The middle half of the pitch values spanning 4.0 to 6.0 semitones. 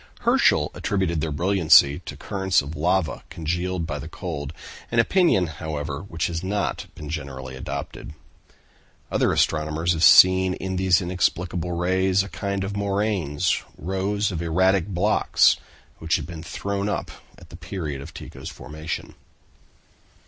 No: average, 3.5 semitones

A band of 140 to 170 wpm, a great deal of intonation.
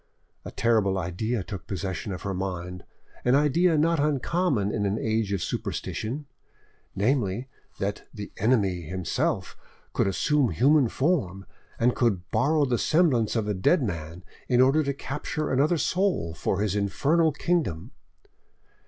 Yes: average, 145 wpm; wide, 7.1 semitones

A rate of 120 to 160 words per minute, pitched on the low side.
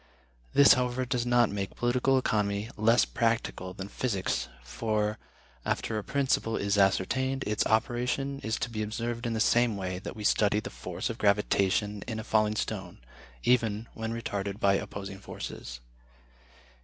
Yes: average, 155 wpm; low, 110 Hz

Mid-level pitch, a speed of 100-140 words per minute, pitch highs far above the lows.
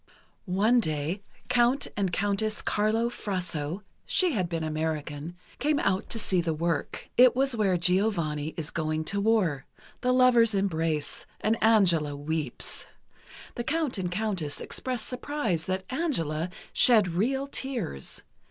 No: high, 195 Hz; slow, 135 wpm; wide, 6.6 semitones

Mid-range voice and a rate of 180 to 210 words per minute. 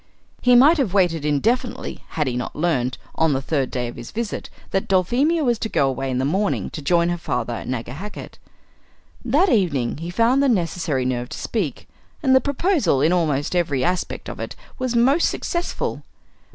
Yes: medium, 175 Hz; average, 190 wpm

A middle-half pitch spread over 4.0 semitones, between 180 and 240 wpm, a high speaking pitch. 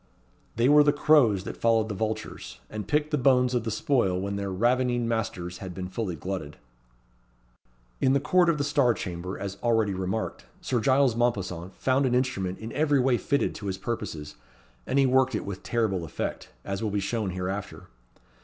No: average, 5.1 semitones; average, 185 wpm; low, 110 Hz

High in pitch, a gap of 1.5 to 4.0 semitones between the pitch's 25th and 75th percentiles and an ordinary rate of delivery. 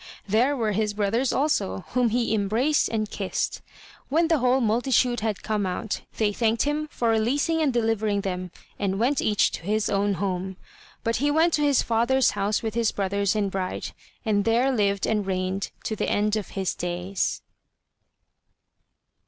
Yes: high, 220 Hz; average, 3.7 semitones; average, 170 wpm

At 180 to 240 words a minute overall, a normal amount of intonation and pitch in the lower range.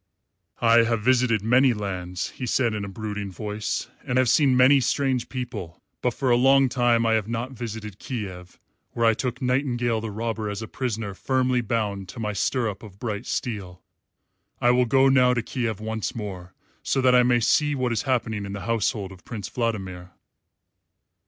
Yes: average, 185 wpm; average, 3.3 semitones; low, 115 Hz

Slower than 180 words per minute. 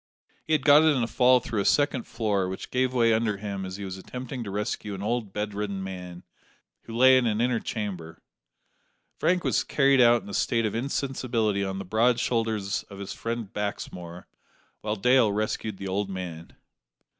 No: average, 190 wpm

